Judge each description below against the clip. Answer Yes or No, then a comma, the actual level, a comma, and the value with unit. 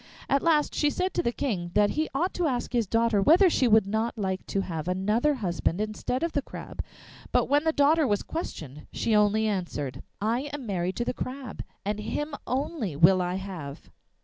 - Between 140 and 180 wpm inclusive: No, average, 200 wpm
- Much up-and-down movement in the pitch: Yes, wide, 7.0 semitones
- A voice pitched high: Yes, high, 220 Hz